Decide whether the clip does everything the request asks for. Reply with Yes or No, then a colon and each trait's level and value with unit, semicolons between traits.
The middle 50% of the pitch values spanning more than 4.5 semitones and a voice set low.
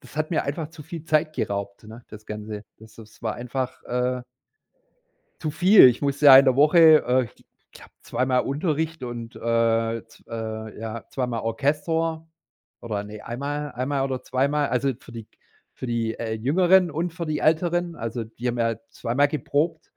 Yes: average, 5.0 semitones; low, 130 Hz